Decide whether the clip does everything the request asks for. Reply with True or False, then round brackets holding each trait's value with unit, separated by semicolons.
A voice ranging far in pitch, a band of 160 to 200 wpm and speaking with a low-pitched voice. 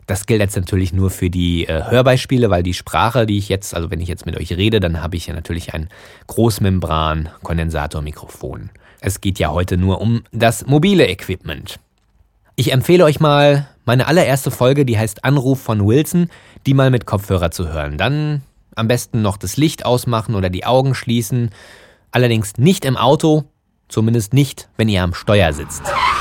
True (5.9 semitones; 180 wpm; 110 Hz)